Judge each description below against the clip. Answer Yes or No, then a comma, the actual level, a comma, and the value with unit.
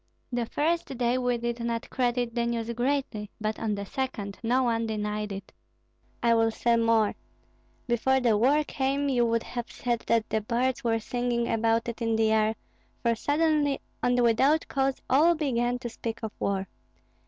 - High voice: Yes, high, 235 Hz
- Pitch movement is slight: Yes, narrow, 2.3 semitones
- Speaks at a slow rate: No, average, 175 wpm